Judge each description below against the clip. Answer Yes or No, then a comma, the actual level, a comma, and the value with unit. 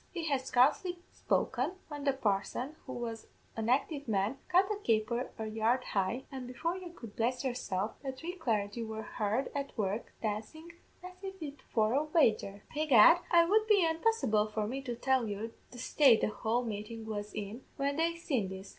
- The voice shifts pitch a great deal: Yes, wide, 6.0 semitones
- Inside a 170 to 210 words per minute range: Yes, average, 185 wpm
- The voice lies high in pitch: Yes, very high, 250 Hz